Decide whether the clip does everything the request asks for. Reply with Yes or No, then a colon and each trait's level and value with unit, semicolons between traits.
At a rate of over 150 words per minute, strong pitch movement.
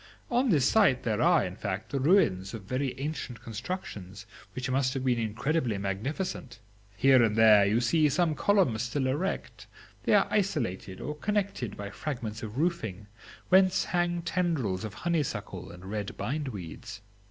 Yes: average, 160 wpm; wide, 7.5 semitones